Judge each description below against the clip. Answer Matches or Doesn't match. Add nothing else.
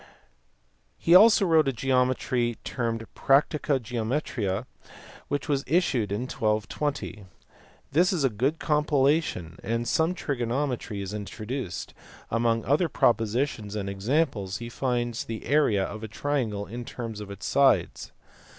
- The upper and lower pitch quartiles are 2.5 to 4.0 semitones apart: Doesn't match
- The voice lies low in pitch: Matches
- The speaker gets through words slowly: Matches